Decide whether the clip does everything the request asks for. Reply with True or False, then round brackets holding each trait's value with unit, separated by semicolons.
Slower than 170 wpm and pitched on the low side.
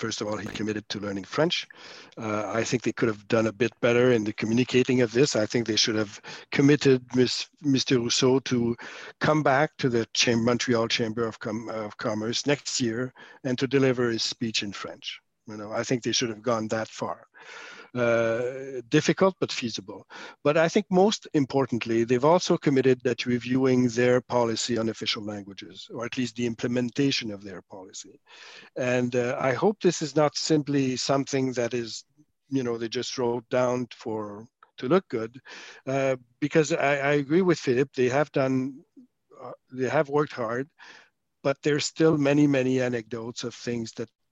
False (185 wpm; 125 Hz)